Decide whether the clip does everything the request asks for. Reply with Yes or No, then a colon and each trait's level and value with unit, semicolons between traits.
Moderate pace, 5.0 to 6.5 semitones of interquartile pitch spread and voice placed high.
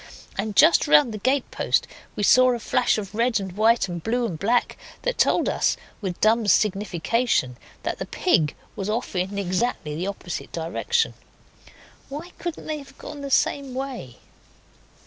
Yes: average, 165 wpm; wide, 5.5 semitones; high, 220 Hz